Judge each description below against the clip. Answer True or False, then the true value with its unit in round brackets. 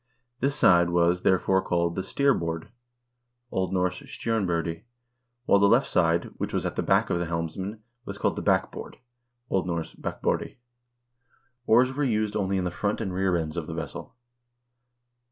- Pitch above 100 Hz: False (95 Hz)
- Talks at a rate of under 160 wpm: False (170 wpm)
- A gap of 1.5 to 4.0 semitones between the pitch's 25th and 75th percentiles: True (3.7 semitones)